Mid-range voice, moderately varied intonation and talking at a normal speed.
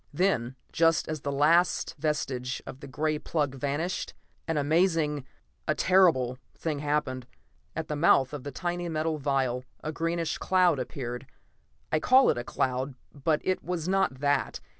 Yes: medium, 150 Hz; average, 3.7 semitones; average, 160 wpm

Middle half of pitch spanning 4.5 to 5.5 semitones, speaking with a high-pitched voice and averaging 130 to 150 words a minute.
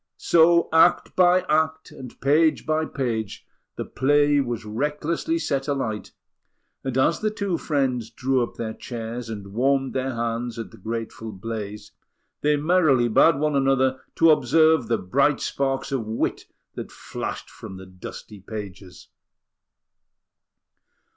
No: average, 5.0 semitones; low, 130 Hz; average, 140 wpm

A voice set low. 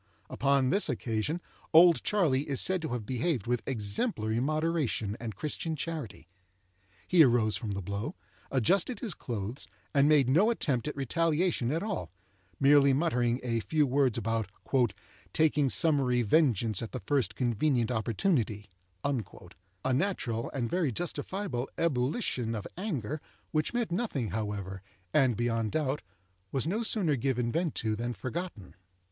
Yes: low, 130 Hz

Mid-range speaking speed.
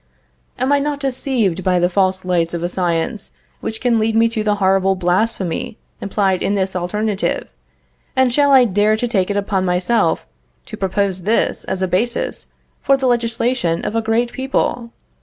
Yes: average, 175 wpm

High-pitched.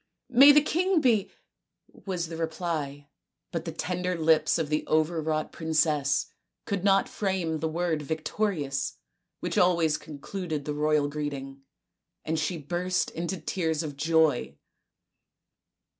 No: medium, 160 Hz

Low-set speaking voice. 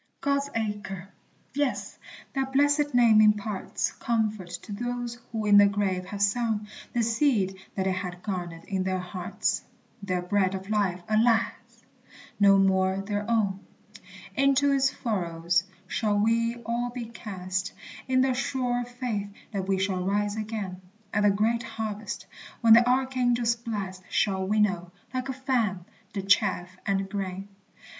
No: high, 210 Hz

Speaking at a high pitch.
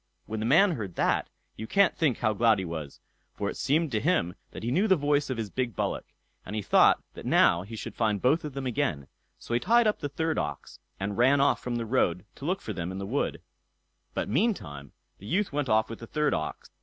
No: low, 120 Hz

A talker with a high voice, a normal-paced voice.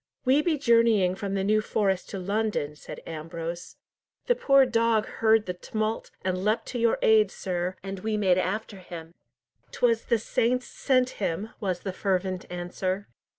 Yes: high, 205 Hz; average, 165 wpm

